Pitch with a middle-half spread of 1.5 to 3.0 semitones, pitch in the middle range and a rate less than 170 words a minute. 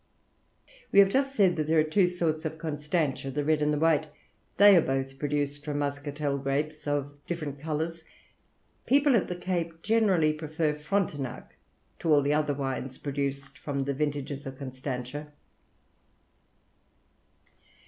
Yes: narrow, 2.6 semitones; medium, 150 Hz; average, 150 wpm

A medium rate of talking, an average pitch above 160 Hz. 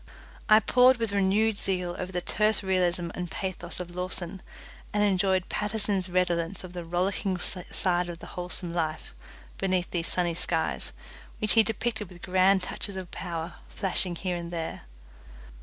Yes: average, 155 wpm; medium, 185 Hz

